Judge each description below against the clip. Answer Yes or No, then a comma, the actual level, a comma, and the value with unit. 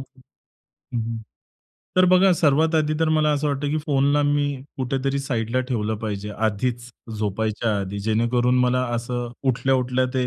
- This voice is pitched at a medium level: No, low, 125 Hz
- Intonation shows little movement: No, average, 4.2 semitones